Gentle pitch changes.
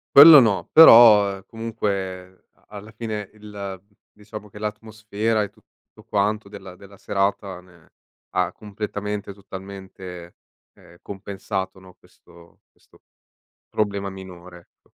Yes: narrow, 2.0 semitones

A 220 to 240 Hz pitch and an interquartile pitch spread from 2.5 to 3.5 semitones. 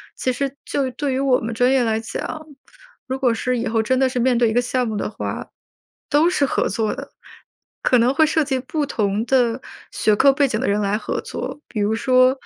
No: very high, 250 Hz; average, 3.1 semitones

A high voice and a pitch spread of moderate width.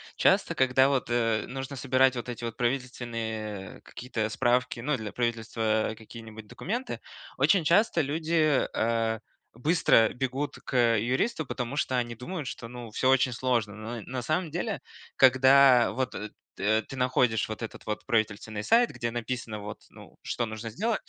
No: low, 120 Hz; average, 3.1 semitones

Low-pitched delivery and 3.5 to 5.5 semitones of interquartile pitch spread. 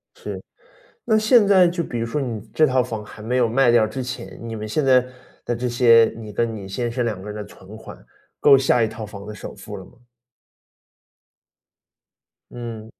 No: low, 115 Hz; average, 3.1 semitones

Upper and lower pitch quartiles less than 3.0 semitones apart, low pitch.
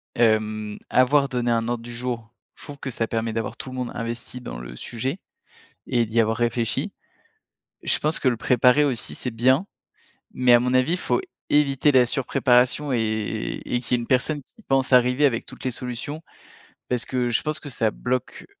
Yes: narrow, 2.4 semitones; low, 125 Hz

